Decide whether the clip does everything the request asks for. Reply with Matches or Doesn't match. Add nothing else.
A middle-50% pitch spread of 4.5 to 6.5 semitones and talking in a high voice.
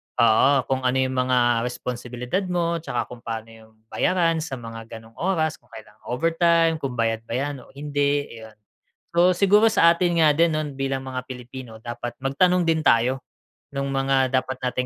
Doesn't match